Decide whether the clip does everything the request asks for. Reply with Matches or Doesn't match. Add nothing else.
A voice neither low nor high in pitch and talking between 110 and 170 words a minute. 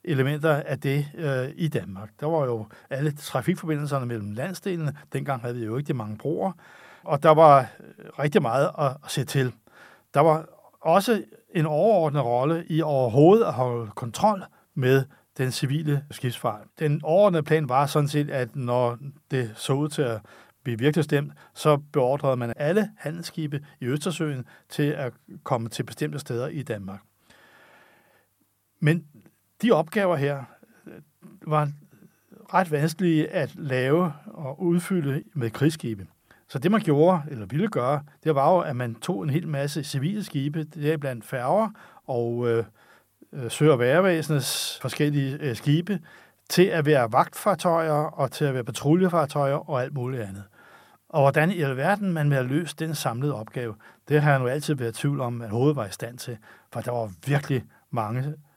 Matches